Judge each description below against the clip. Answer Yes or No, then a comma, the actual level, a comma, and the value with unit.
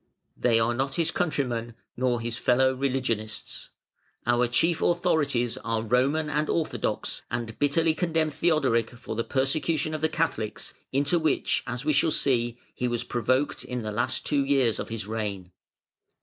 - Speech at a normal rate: Yes, average, 160 wpm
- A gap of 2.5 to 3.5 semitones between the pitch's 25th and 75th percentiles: No, average, 4.5 semitones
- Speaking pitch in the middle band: No, low, 130 Hz